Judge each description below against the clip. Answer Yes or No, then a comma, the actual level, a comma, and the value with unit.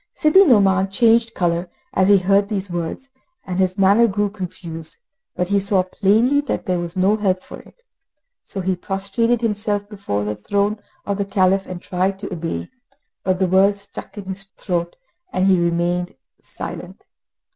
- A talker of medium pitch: No, high, 195 Hz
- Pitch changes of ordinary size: No, narrow, 2.1 semitones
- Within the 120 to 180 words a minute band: Yes, average, 170 wpm